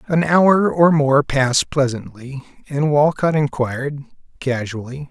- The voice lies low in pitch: No, medium, 145 Hz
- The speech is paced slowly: Yes, slow, 120 wpm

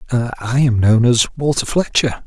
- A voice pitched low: Yes, low, 125 Hz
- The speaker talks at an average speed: Yes, average, 160 wpm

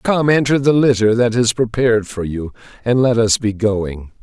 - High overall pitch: No, low, 115 Hz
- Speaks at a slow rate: No, average, 200 wpm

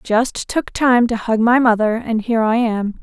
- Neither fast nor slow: No, fast, 220 wpm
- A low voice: No, high, 230 Hz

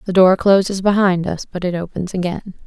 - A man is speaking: No, female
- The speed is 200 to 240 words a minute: Yes, fast, 205 wpm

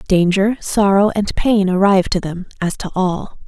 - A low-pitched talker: No, high, 195 Hz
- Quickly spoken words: No, average, 175 wpm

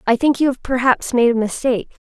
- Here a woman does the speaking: Yes, female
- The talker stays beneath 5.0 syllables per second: No, 6.0 syllables/s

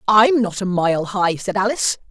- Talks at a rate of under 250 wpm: Yes, average, 200 wpm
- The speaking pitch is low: No, high, 200 Hz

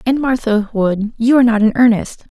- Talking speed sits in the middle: Yes, average, 180 wpm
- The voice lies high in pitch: Yes, high, 230 Hz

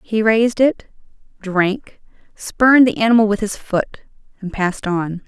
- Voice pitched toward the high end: Yes, high, 210 Hz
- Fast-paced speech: No, average, 150 wpm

